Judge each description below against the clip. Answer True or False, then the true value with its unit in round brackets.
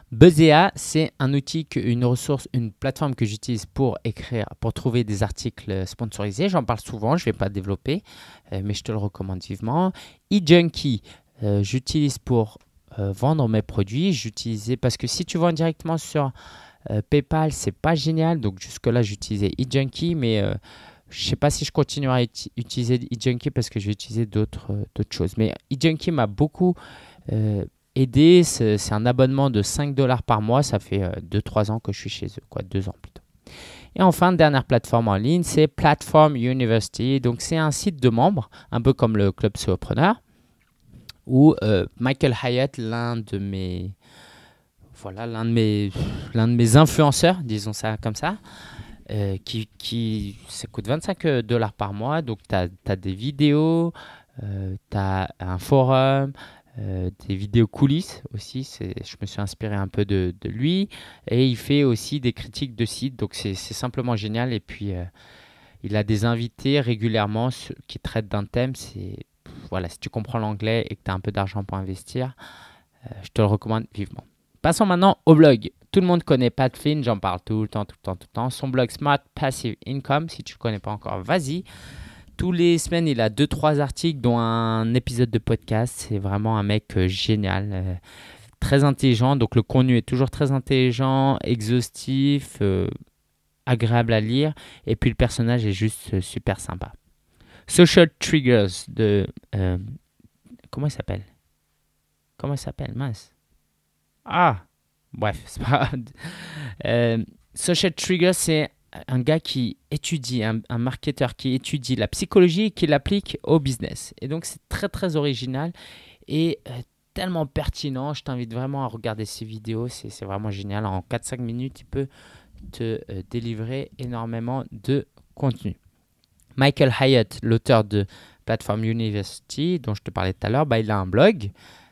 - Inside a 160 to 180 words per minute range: True (175 wpm)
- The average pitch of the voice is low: True (120 Hz)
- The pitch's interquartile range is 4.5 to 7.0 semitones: True (5.1 semitones)